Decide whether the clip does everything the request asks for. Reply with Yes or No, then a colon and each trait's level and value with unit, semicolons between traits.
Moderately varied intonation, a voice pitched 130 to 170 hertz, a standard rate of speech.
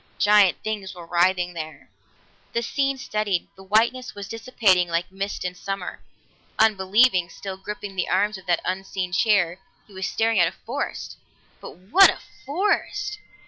No: average, 3.3 semitones; high, 195 Hz; average, 155 wpm